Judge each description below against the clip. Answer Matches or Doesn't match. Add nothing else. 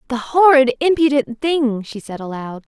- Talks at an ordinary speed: Matches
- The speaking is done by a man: Doesn't match